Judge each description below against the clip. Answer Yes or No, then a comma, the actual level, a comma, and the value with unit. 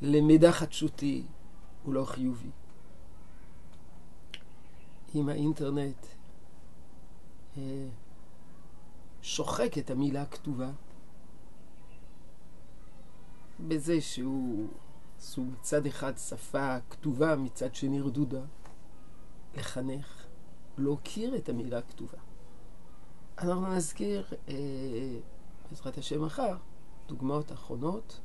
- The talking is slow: Yes, slow, 75 wpm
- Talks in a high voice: No, low, 135 Hz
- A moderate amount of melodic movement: No, wide, 7.9 semitones